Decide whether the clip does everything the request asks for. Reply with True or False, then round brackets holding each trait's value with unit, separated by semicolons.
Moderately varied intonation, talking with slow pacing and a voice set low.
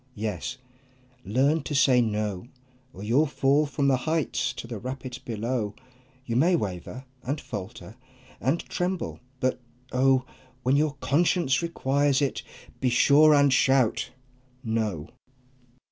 True (3.8 semitones; 130 wpm; 130 Hz)